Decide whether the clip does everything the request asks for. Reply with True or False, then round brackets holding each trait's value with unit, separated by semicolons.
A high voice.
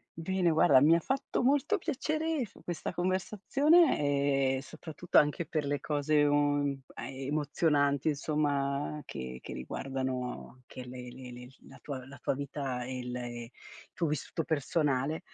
False (145 Hz)